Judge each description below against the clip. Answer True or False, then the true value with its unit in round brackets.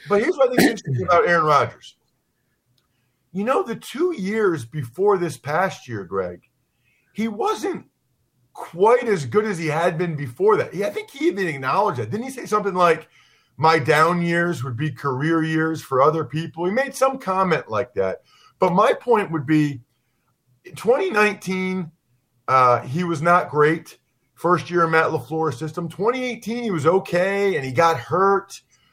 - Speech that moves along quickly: False (175 wpm)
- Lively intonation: True (5.7 semitones)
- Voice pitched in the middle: True (170 Hz)